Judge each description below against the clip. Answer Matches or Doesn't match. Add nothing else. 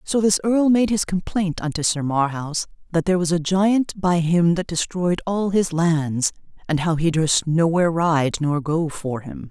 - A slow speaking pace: Doesn't match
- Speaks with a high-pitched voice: Doesn't match